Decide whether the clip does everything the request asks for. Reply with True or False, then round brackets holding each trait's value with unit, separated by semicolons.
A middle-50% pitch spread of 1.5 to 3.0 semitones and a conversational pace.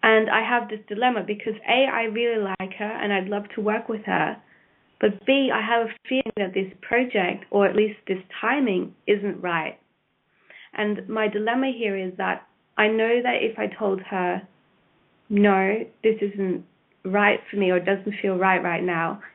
True (2.5 semitones; 185 wpm)